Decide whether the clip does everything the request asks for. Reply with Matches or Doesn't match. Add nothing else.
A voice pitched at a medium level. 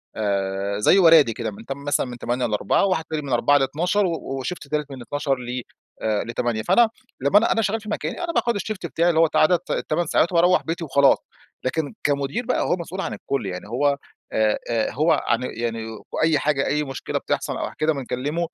Matches